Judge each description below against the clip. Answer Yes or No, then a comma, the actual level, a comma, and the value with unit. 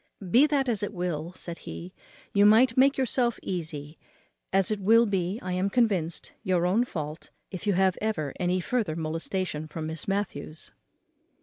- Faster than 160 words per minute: Yes, average, 170 wpm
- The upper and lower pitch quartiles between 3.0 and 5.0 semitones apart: Yes, average, 4.6 semitones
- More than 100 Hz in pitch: Yes, medium, 185 Hz